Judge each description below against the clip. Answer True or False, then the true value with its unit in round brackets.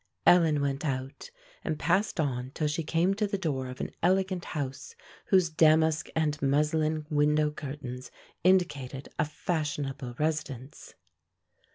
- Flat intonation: False (3.0 semitones)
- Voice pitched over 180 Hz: False (150 Hz)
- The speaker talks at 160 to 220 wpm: False (135 wpm)